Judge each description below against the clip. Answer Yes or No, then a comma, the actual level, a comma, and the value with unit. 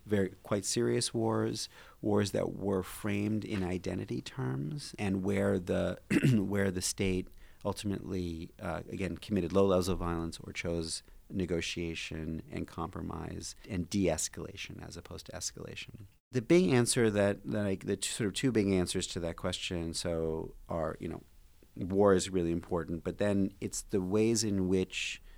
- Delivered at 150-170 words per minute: Yes, average, 160 wpm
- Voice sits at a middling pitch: No, very low, 95 Hz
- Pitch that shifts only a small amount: No, average, 3.1 semitones